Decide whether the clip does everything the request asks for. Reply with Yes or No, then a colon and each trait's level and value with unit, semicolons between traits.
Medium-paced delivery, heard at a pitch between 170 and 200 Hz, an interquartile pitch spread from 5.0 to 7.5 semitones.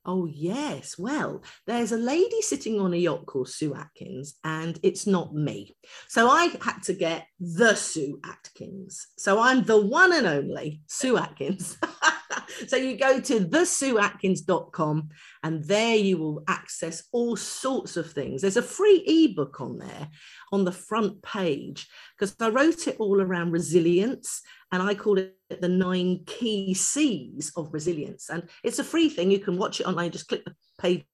Yes: average, 170 wpm; high, 190 Hz; wide, 5.5 semitones